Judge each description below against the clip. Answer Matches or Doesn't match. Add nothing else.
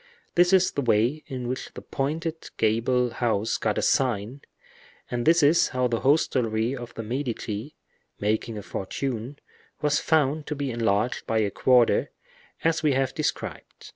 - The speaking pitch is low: Matches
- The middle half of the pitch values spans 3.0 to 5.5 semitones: Matches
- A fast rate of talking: Doesn't match